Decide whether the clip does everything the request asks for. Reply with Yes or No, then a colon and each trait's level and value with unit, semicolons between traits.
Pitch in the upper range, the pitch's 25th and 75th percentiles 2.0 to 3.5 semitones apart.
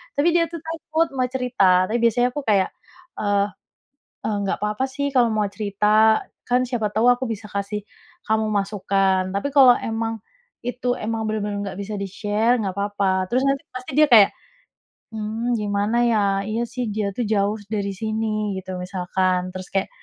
Yes: high, 215 Hz; average, 3.2 semitones